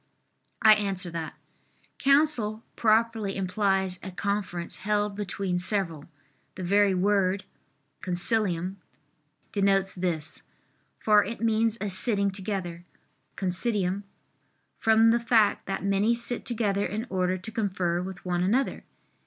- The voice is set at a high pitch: Yes, high, 200 Hz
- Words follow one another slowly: Yes, slow, 120 wpm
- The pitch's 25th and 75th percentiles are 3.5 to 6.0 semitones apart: No, average, 2.9 semitones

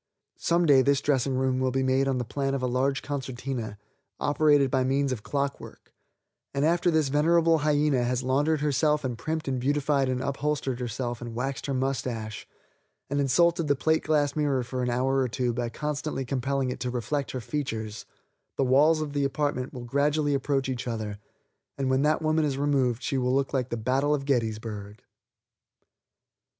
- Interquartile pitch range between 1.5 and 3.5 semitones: Yes, narrow, 2.5 semitones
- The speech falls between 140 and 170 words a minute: No, average, 185 wpm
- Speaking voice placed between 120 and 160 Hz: Yes, low, 135 Hz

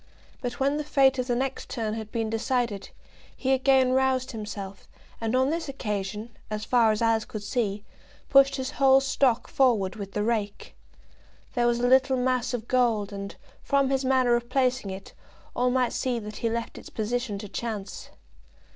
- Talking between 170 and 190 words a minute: Yes, average, 180 wpm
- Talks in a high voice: Yes, high, 240 Hz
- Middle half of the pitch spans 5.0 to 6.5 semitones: No, average, 3.5 semitones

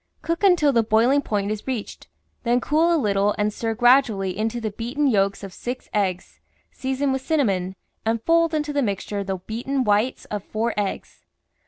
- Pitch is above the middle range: Yes, high, 230 Hz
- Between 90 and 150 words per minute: No, average, 185 wpm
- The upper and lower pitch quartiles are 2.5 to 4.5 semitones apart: No, average, 4.9 semitones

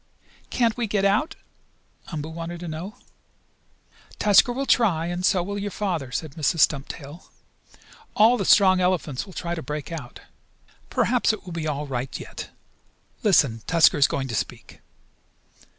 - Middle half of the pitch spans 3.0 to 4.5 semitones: No, average, 5.2 semitones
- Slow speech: No, average, 155 wpm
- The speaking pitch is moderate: Yes, medium, 175 Hz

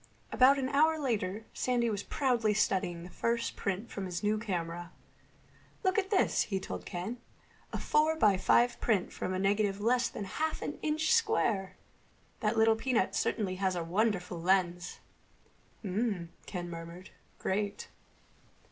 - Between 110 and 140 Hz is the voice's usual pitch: No, high, 210 Hz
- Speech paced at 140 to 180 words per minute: Yes, average, 150 wpm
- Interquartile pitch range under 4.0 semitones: No, average, 4.8 semitones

